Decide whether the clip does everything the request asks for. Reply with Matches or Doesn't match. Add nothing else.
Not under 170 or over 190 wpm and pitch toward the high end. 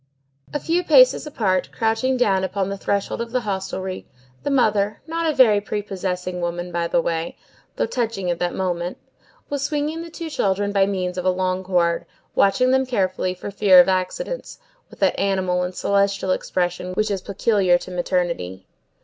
Matches